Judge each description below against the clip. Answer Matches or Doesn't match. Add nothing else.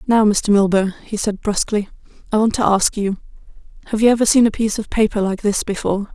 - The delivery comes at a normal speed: Doesn't match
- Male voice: Doesn't match